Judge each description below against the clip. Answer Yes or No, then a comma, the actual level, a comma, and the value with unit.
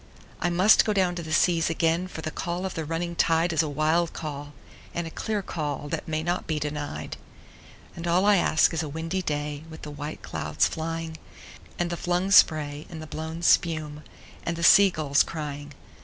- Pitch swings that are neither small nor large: No, narrow, 2.2 semitones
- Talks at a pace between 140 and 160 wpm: No, average, 200 wpm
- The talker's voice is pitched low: No, medium, 165 Hz